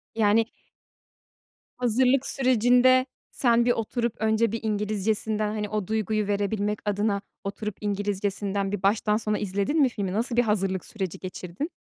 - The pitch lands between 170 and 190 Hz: No, high, 215 Hz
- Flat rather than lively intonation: Yes, narrow, 2.3 semitones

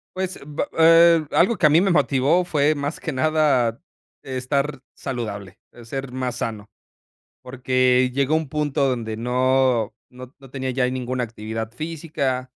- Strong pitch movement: No, average, 3.3 semitones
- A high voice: No, low, 130 Hz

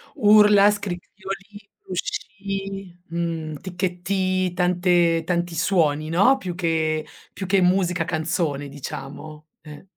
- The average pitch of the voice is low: No, medium, 180 Hz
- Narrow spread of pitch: No, average, 3.1 semitones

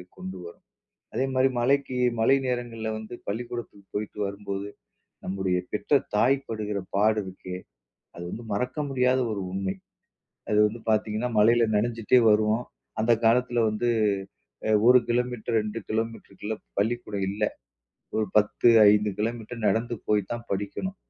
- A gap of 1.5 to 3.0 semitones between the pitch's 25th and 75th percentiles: Yes, average, 2.7 semitones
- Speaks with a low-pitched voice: Yes, low, 110 Hz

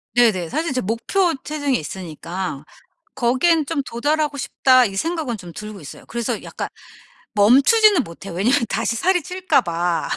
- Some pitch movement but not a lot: No, wide, 8.2 semitones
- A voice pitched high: Yes, high, 245 Hz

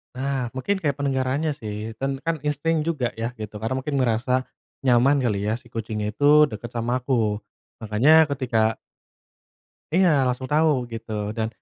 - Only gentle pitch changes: No, average, 4.3 semitones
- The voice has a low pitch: Yes, low, 130 Hz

